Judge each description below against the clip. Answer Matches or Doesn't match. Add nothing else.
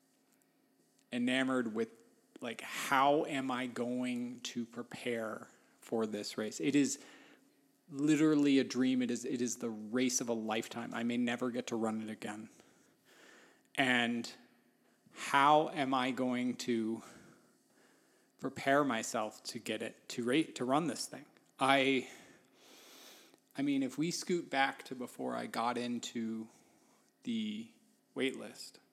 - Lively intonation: Doesn't match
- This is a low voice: Matches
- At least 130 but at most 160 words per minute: Matches